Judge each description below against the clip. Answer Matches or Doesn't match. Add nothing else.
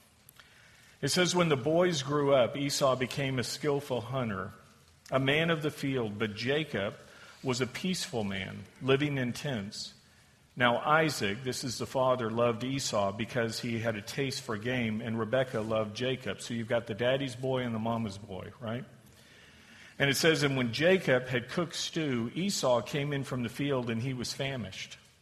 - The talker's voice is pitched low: Matches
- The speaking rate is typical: Matches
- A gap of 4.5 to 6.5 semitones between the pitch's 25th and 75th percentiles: Doesn't match